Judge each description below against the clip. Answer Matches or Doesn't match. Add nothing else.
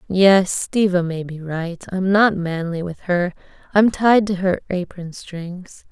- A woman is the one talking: Matches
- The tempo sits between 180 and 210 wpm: Doesn't match